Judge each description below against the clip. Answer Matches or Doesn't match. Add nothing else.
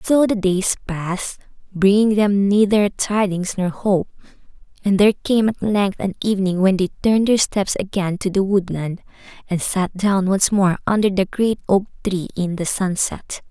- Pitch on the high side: Matches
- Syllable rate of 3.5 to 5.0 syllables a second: Matches